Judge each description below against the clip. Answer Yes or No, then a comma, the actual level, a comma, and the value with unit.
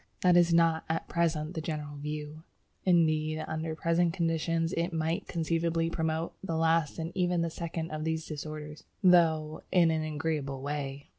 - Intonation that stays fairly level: Yes, narrow, 1.5 semitones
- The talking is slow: No, average, 160 wpm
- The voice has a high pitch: No, medium, 160 Hz